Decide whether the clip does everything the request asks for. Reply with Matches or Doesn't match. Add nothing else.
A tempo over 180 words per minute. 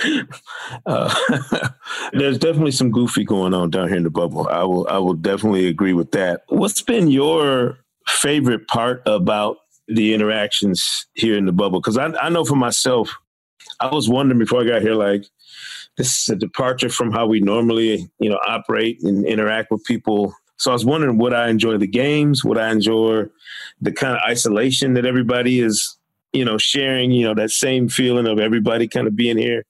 Matches